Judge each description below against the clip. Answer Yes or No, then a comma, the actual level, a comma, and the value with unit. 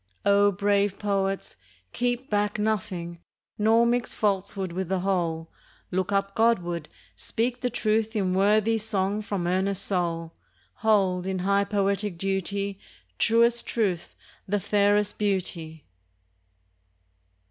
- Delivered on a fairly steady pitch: Yes, narrow, 2.3 semitones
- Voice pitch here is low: No, high, 200 Hz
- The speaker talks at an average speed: No, slow, 115 wpm